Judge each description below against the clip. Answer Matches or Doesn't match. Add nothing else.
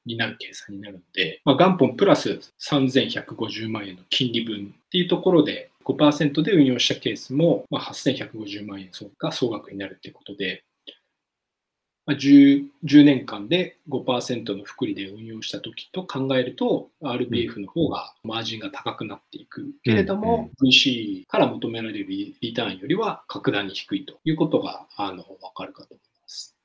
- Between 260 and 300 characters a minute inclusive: Matches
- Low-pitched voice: Matches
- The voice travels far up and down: Matches